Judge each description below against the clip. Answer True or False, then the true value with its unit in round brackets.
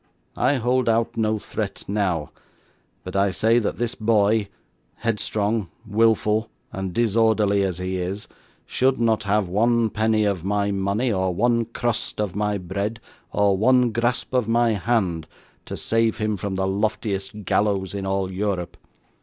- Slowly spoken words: False (155 wpm)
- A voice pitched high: False (105 Hz)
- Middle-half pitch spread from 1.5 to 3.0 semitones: True (2.7 semitones)